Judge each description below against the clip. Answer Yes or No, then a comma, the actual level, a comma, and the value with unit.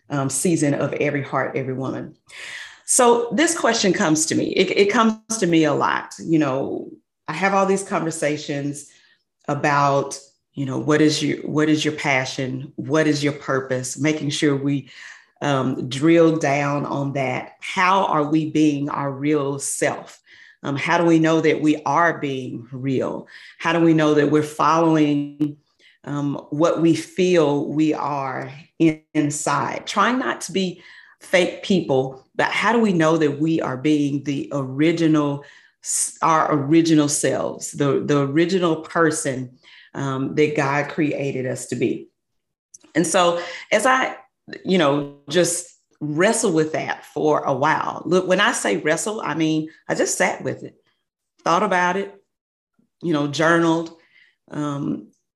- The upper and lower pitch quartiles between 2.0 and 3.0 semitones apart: Yes, average, 2.7 semitones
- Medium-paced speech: Yes, average, 155 wpm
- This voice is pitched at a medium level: Yes, medium, 150 Hz